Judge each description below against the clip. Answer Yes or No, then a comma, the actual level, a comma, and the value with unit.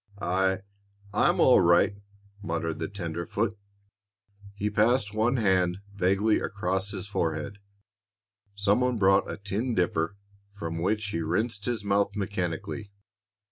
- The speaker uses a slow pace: Yes, slow, 125 wpm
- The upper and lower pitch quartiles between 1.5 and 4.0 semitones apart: Yes, average, 2.9 semitones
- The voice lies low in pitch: Yes, low, 100 Hz